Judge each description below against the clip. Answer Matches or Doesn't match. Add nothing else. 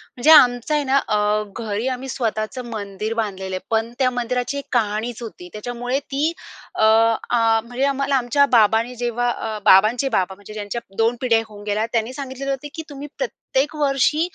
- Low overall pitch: Doesn't match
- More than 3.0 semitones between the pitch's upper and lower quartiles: Matches